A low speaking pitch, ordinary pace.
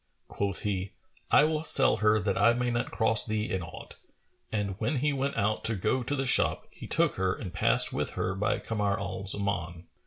No: low, 105 Hz; fast, 210 wpm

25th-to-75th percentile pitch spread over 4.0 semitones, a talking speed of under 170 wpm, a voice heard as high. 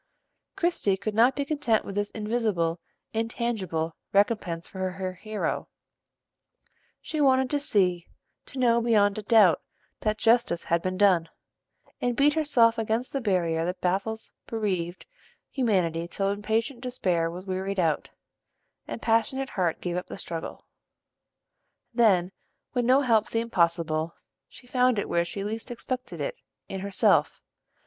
Yes: average, 4.7 semitones; average, 140 wpm; high, 210 Hz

